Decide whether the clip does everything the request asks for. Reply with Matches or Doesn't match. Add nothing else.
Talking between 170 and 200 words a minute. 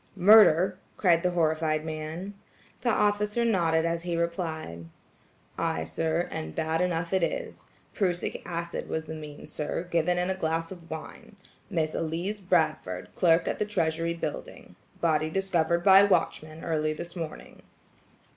Doesn't match